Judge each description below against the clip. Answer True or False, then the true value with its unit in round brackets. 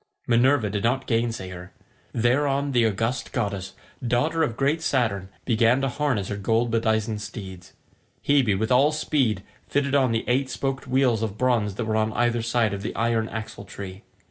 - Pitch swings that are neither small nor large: True (3.6 semitones)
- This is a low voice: True (115 Hz)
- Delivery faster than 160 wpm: True (175 wpm)